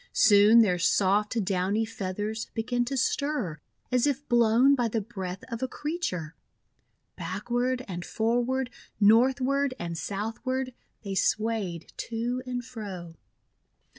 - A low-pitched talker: No, high, 225 Hz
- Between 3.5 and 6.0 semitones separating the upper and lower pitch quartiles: Yes, average, 4.5 semitones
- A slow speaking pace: Yes, slow, 125 wpm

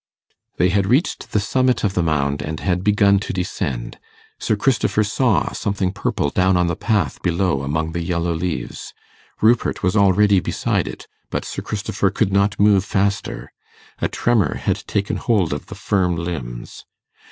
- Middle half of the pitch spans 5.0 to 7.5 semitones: No, average, 3.4 semitones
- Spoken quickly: No, average, 165 wpm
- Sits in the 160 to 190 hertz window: No, very low, 95 Hz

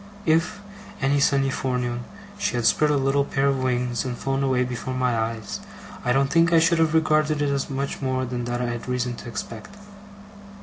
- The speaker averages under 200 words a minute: No, fast, 205 wpm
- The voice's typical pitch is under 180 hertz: Yes, low, 135 Hz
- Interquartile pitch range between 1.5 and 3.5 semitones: Yes, average, 2.9 semitones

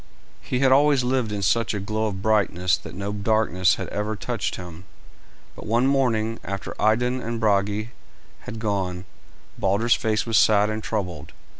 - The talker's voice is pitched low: Yes, low, 110 Hz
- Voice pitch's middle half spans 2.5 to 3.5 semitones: Yes, average, 2.8 semitones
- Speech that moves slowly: No, average, 165 wpm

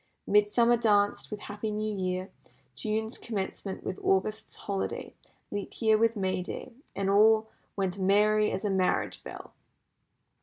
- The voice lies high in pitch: Yes, high, 205 Hz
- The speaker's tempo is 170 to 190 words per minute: No, average, 140 wpm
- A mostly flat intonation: Yes, narrow, 2.0 semitones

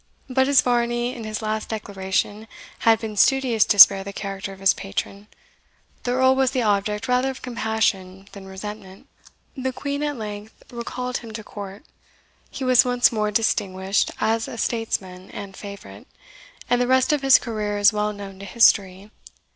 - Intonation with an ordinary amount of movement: Yes, average, 3.7 semitones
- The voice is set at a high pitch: Yes, high, 215 Hz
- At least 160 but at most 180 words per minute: Yes, average, 170 wpm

